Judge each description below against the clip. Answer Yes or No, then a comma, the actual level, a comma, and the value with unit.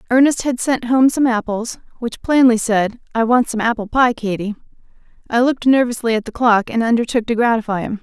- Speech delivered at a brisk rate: No, average, 195 wpm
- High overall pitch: Yes, high, 235 Hz